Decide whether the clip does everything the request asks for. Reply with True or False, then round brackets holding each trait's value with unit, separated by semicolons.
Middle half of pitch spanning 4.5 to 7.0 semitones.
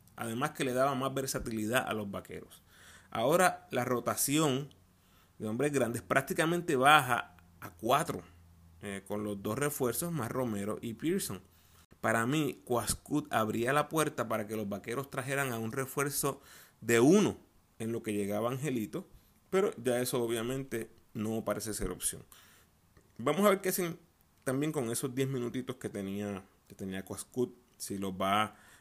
True (5.3 semitones)